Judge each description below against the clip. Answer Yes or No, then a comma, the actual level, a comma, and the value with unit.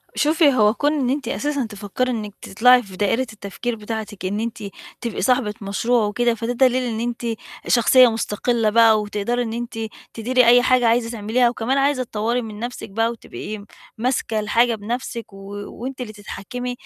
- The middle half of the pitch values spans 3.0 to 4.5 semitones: No, narrow, 2.6 semitones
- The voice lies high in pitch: Yes, high, 235 Hz